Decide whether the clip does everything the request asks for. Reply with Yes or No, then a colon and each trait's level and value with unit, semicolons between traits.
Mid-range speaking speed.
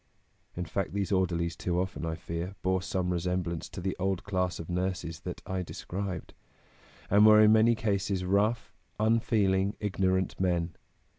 Yes: average, 160 wpm